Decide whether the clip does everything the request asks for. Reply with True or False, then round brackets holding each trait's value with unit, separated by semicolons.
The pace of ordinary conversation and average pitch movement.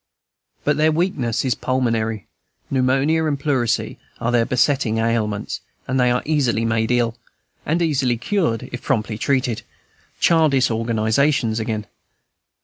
False (125 wpm; 3.8 semitones)